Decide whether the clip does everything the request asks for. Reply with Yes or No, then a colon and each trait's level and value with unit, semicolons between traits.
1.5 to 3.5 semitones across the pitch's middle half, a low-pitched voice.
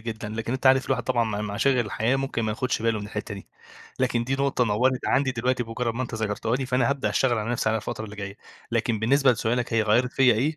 Yes: average, 2.8 semitones; low, 120 Hz